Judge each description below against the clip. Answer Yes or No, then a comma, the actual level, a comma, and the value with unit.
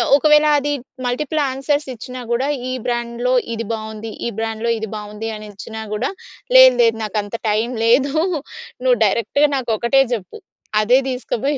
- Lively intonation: No, average, 3.5 semitones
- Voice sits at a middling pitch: No, high, 235 Hz